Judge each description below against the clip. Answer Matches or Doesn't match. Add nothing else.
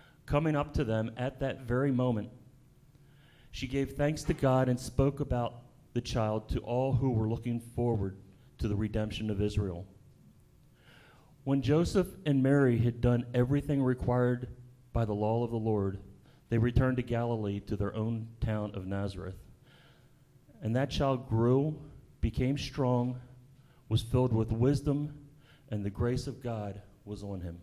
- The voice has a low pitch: Matches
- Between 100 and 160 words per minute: Matches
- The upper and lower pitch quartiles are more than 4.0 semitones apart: Doesn't match